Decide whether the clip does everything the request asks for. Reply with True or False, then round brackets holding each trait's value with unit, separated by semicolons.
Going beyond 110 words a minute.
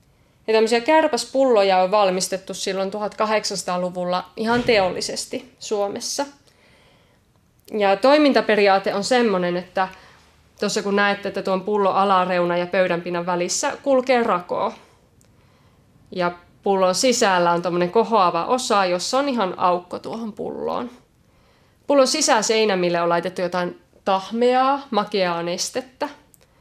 False (100 wpm)